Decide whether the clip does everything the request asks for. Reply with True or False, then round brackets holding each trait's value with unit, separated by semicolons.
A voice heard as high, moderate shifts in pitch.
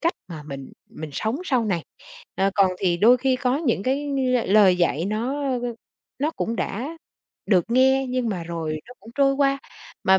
False (235 Hz; 6.1 semitones)